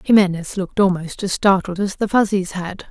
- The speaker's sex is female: Yes, female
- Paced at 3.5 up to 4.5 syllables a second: No, 5.4 syllables/s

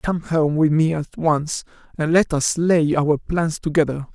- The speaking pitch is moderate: Yes, medium, 155 Hz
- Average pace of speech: Yes, average, 190 wpm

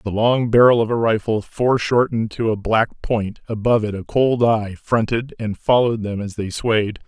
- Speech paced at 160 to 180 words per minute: No, average, 195 wpm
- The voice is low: Yes, low, 110 Hz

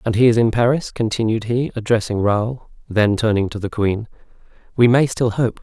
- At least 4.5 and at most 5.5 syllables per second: Yes, 5.2 syllables/s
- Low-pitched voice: Yes, low, 115 Hz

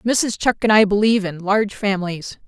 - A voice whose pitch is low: No, high, 205 Hz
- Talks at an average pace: Yes, average, 195 wpm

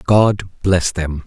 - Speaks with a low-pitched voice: Yes, very low, 90 Hz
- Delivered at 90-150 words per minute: Yes, average, 140 wpm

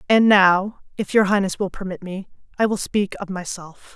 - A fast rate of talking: No, average, 195 wpm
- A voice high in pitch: Yes, high, 195 Hz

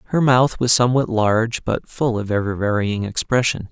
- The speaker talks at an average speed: Yes, average, 180 wpm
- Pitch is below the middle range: Yes, low, 115 Hz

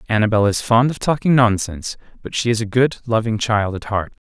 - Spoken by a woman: No, male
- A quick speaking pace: Yes, fast, 210 wpm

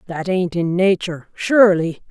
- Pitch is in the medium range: Yes, medium, 180 Hz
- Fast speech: No, average, 140 wpm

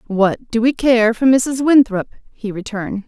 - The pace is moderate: Yes, average, 175 wpm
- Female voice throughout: Yes, female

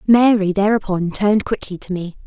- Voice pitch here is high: Yes, high, 200 Hz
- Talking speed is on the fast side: No, average, 160 wpm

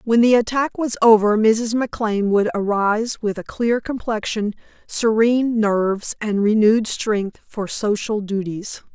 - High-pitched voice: Yes, high, 215 Hz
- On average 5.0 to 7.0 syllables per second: No, 4.5 syllables/s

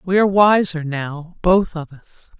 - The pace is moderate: Yes, average, 175 wpm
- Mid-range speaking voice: Yes, medium, 175 Hz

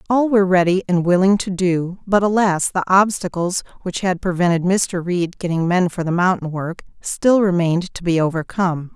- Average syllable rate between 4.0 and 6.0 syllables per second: Yes, 5.1 syllables/s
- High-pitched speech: No, medium, 180 Hz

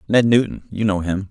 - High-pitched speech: No, low, 105 Hz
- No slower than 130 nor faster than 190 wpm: No, fast, 230 wpm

